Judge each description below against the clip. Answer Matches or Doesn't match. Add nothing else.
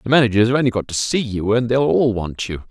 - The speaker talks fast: Matches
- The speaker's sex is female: Doesn't match